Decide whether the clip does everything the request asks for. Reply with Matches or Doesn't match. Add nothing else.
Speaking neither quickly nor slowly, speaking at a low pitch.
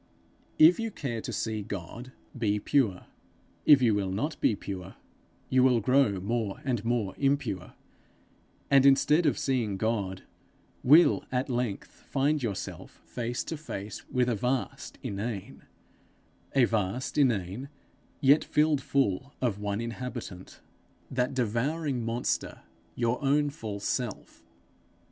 Doesn't match